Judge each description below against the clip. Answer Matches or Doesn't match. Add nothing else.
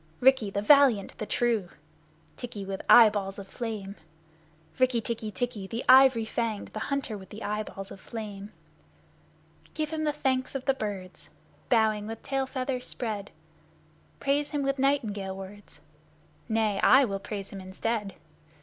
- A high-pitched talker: Matches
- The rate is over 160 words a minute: Doesn't match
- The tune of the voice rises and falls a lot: Doesn't match